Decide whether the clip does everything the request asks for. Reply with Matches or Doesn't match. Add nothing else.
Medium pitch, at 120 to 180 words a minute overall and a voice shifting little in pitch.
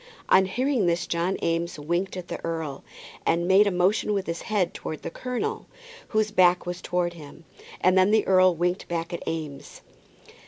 Doesn't match